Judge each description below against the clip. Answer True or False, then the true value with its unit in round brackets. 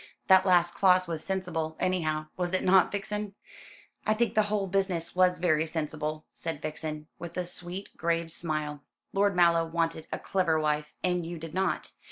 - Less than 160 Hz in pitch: False (175 Hz)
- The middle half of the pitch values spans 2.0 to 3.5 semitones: True (2.9 semitones)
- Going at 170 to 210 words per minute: True (175 wpm)